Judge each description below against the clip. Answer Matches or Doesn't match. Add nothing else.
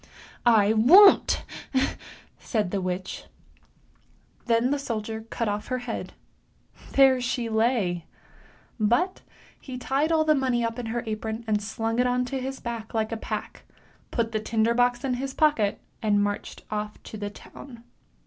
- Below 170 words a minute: Matches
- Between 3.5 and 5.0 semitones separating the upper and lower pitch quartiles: Doesn't match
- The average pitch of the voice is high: Matches